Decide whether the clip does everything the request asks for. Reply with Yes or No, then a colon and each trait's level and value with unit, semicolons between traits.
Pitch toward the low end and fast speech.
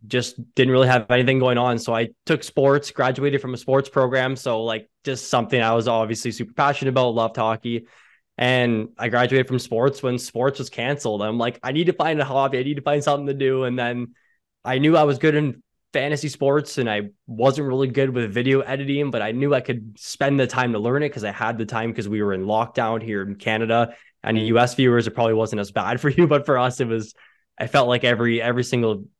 Yes: low, 125 Hz; fast, 240 wpm